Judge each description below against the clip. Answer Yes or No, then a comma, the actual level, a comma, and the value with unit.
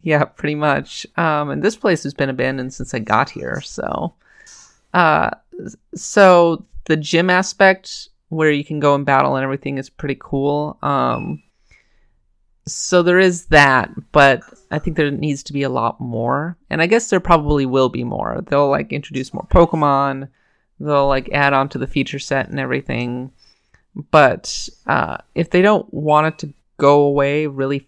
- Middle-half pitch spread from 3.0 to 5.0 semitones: Yes, average, 3.3 semitones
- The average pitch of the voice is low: No, medium, 145 Hz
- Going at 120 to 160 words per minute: No, average, 170 wpm